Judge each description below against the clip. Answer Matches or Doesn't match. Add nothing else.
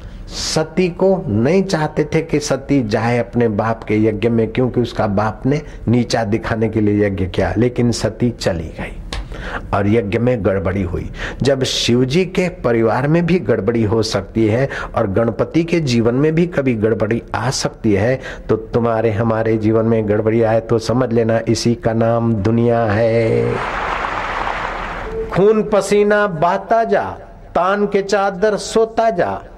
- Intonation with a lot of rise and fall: Matches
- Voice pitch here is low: Matches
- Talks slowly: Doesn't match